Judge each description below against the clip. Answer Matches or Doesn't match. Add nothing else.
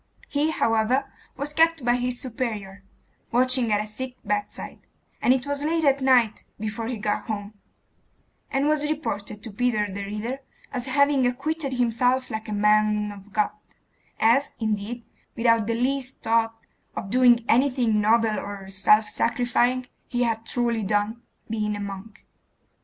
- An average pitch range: Matches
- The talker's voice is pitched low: Doesn't match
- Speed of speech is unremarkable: Matches